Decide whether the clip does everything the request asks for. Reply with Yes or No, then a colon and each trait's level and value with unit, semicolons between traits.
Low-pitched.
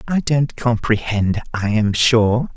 Yes: low, 115 Hz